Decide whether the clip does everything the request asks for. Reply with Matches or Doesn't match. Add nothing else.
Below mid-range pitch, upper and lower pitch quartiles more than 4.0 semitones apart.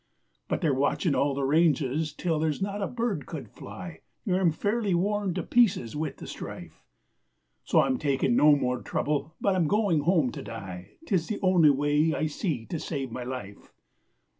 Doesn't match